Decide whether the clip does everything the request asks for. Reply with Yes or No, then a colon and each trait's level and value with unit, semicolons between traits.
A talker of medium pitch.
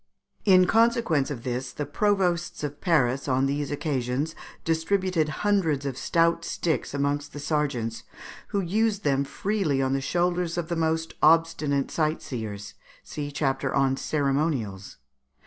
Yes: medium, 150 Hz